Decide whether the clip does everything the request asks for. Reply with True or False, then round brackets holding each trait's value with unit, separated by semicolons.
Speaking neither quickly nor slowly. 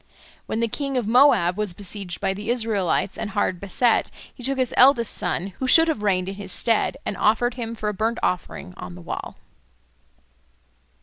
True (190 wpm)